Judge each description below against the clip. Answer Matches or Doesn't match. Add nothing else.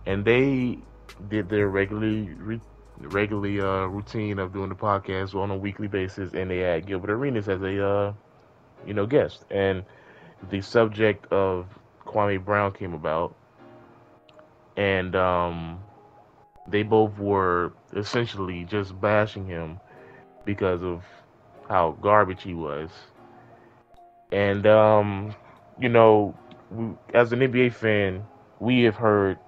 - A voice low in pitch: Matches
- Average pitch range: Doesn't match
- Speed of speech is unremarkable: Doesn't match